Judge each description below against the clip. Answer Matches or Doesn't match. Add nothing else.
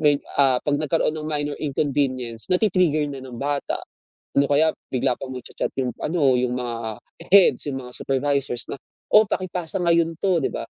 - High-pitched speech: Doesn't match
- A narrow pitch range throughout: Doesn't match